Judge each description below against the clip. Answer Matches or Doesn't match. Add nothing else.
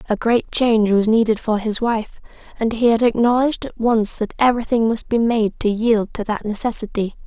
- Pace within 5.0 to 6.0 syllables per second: Matches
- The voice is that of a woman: Matches